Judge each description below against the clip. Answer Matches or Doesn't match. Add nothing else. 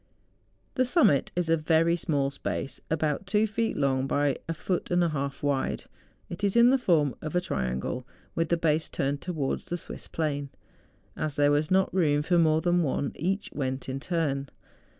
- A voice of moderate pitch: Matches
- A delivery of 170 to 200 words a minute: Matches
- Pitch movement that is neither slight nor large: Matches